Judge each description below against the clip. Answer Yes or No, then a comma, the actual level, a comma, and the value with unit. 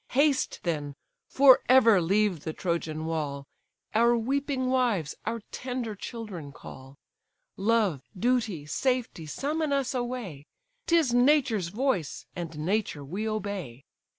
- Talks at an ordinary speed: No, slow, 120 wpm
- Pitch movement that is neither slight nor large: No, wide, 7.7 semitones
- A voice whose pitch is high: Yes, high, 215 Hz